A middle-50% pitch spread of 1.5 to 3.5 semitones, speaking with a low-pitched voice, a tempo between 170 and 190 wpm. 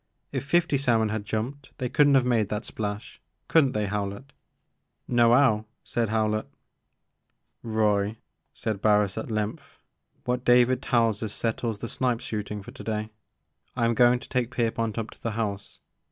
Yes: narrow, 2.6 semitones; low, 115 Hz; average, 175 wpm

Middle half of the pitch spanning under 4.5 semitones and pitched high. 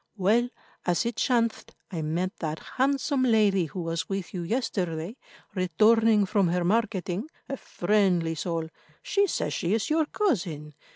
No: average, 5.2 semitones; high, 195 Hz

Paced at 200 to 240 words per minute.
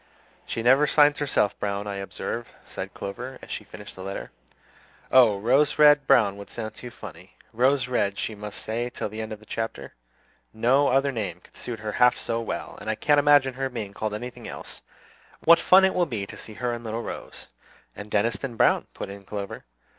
Yes: fast, 205 wpm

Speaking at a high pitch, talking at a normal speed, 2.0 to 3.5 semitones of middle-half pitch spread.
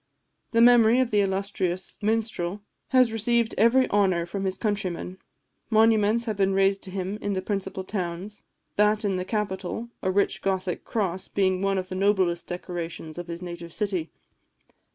Yes: high, 195 Hz; average, 165 wpm; narrow, 2.5 semitones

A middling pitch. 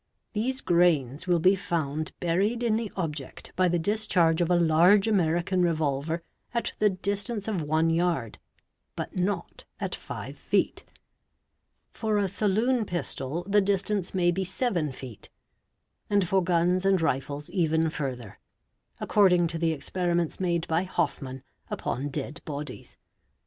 Yes: medium, 175 Hz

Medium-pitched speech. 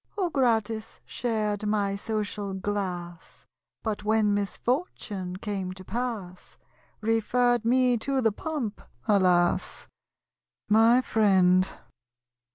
No: high, 210 Hz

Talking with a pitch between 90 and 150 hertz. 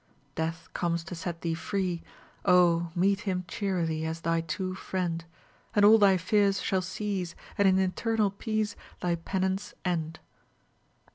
No: medium, 185 Hz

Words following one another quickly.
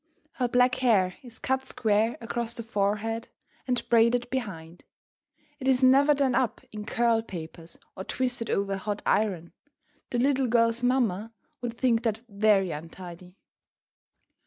No: average, 145 wpm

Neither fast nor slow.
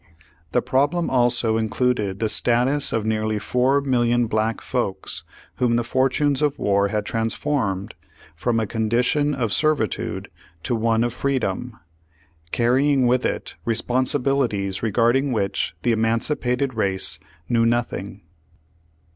No: slow, 125 wpm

